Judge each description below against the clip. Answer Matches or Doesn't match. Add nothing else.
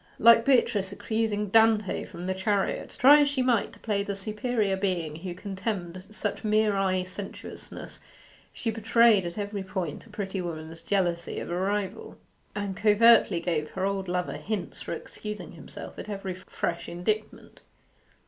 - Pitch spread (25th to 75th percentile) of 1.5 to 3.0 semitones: Matches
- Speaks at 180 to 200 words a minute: Doesn't match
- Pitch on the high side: Matches